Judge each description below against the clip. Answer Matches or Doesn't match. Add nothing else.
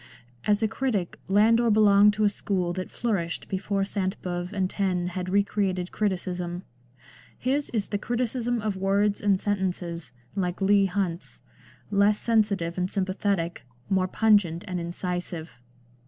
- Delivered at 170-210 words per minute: Doesn't match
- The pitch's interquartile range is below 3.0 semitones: Matches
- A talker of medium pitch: Doesn't match